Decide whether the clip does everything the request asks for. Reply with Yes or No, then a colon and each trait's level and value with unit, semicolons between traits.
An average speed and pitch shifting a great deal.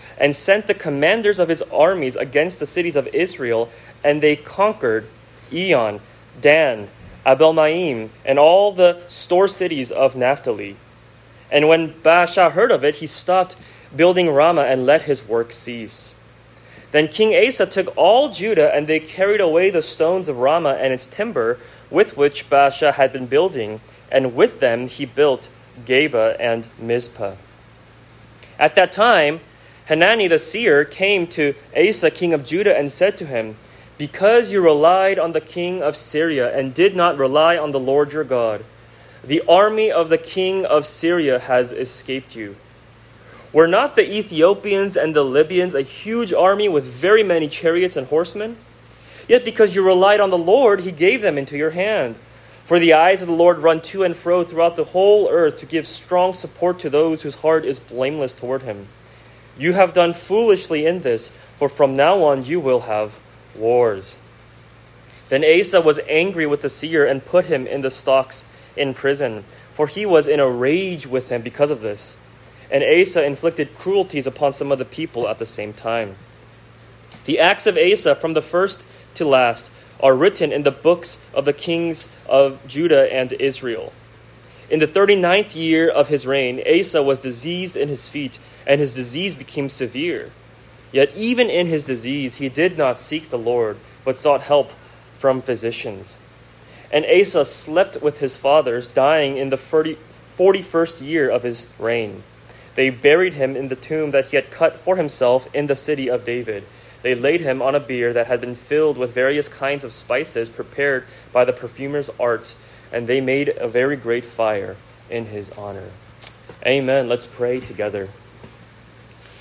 Yes: average, 170 wpm; wide, 5.8 semitones